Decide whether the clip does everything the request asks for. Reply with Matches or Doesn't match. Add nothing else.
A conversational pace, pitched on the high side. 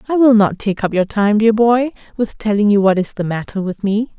Doesn't match